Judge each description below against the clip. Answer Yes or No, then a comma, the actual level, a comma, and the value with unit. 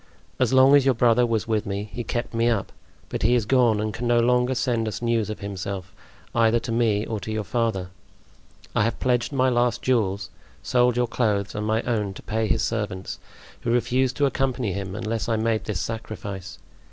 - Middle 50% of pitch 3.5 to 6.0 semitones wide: No, average, 2.7 semitones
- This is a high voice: No, low, 115 Hz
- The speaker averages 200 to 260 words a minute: Yes, fast, 205 wpm